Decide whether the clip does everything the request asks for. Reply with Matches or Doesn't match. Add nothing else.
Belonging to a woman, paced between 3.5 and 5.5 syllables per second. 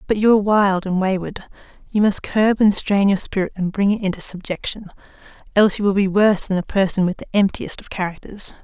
Doesn't match